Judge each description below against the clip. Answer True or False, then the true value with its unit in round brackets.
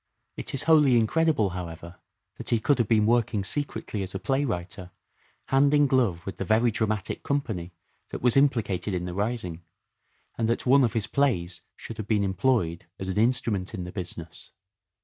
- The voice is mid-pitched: False (110 Hz)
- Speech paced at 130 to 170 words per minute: False (180 wpm)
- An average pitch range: False (5.7 semitones)